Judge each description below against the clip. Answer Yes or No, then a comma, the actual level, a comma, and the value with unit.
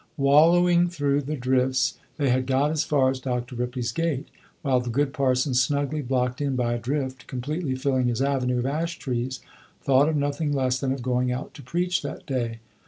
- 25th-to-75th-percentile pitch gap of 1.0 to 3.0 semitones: Yes, narrow, 2.4 semitones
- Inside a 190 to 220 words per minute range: Yes, average, 195 wpm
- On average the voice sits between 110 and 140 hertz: Yes, low, 135 Hz